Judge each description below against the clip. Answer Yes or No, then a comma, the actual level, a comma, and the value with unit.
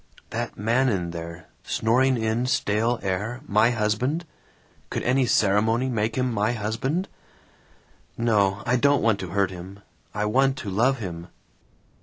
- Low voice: Yes, low, 110 Hz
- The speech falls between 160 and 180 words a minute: No, average, 145 wpm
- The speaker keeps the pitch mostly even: No, average, 3.9 semitones